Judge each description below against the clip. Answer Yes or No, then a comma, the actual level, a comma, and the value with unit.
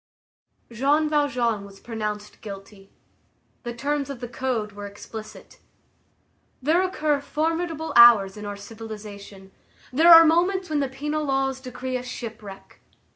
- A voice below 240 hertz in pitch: No, very high, 250 Hz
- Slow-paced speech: Yes, slow, 130 wpm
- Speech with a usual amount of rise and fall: No, wide, 6.0 semitones